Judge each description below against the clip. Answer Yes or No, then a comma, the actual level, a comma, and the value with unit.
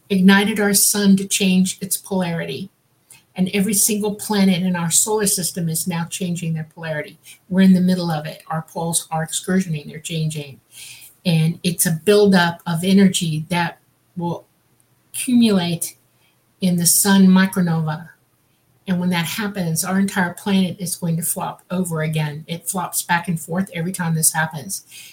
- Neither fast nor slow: Yes, average, 160 wpm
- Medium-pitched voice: Yes, medium, 175 Hz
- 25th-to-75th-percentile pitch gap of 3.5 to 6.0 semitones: No, average, 2.8 semitones